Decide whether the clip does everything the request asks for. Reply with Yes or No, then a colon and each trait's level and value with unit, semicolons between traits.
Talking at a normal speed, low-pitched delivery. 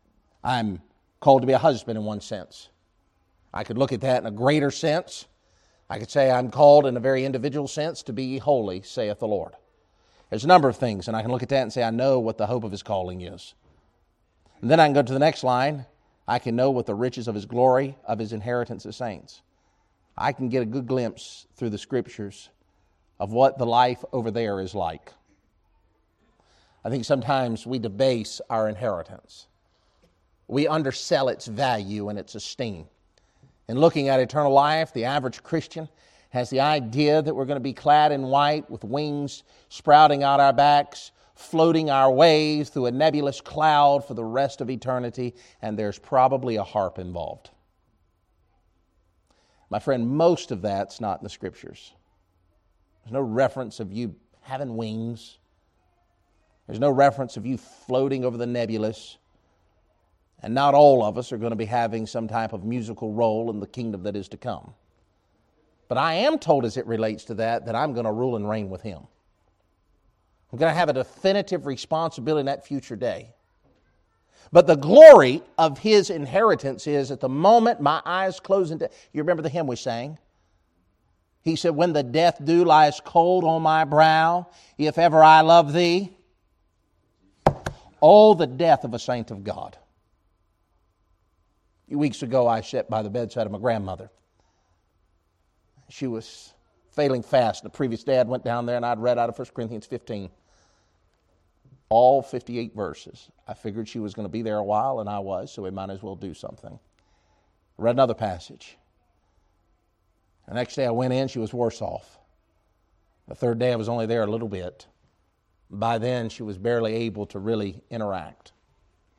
Yes: average, 180 wpm; low, 115 Hz